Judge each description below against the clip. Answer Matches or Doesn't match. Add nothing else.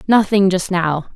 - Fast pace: Doesn't match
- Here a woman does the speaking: Matches